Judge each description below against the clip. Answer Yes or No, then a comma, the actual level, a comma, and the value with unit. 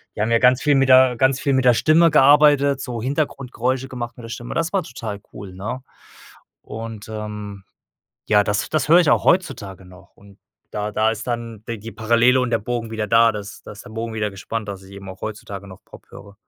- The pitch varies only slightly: No, average, 3.9 semitones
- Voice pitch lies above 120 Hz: No, low, 115 Hz